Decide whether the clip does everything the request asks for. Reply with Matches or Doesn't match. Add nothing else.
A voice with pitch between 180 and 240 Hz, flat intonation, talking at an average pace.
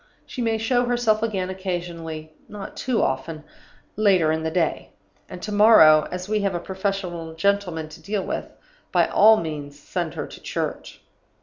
Doesn't match